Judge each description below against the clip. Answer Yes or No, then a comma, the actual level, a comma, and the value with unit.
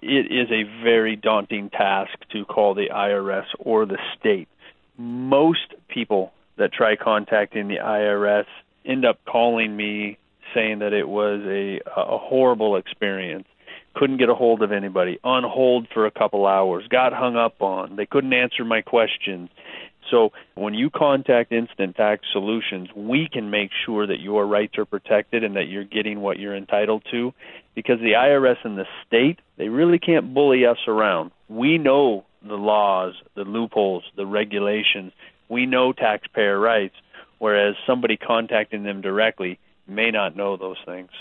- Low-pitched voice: Yes, low, 105 Hz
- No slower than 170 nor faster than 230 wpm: No, average, 160 wpm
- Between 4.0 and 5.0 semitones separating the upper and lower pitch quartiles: No, average, 2.9 semitones